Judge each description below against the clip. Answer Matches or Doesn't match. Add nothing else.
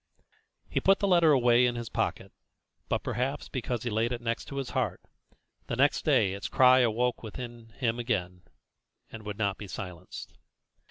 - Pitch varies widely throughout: Doesn't match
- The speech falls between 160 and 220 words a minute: Matches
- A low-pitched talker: Matches